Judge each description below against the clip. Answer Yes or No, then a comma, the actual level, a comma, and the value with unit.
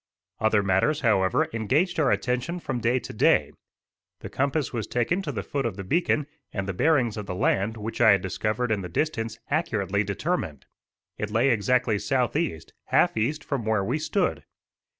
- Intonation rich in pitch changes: Yes, wide, 5.8 semitones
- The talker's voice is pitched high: No, low, 115 Hz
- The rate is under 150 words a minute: No, average, 180 wpm